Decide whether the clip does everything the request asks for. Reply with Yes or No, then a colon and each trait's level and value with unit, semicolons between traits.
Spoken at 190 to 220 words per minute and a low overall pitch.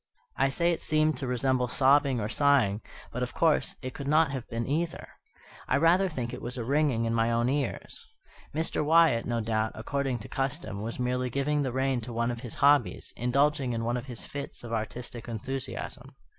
Yes: average, 200 wpm; low, 130 Hz